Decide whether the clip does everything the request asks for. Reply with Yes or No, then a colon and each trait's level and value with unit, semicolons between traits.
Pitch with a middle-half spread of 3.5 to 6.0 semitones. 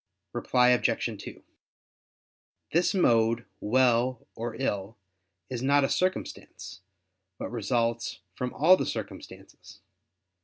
No: narrow, 2.4 semitones